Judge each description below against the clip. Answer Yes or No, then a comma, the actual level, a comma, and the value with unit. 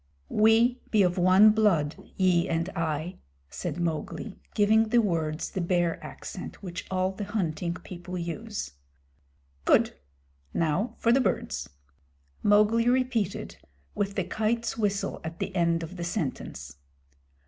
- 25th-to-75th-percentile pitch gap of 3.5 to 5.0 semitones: Yes, average, 4.1 semitones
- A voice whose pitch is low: No, medium, 185 Hz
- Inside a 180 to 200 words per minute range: No, slow, 135 wpm